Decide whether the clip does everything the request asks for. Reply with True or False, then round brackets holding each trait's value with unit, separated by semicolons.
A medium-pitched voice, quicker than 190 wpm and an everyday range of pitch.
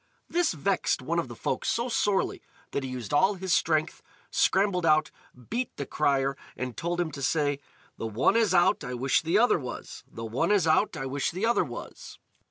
False (160 Hz; 200 wpm; 6.2 semitones)